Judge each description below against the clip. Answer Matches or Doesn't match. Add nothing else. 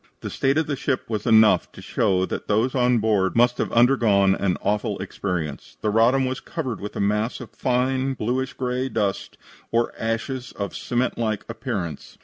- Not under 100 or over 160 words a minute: Doesn't match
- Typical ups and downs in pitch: Matches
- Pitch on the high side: Doesn't match